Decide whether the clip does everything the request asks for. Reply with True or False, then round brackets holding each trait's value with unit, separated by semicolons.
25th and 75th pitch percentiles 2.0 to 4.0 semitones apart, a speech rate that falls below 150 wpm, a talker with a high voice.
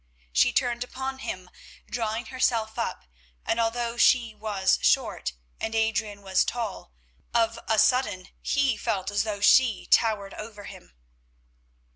True (2.7 semitones; 135 wpm; 220 Hz)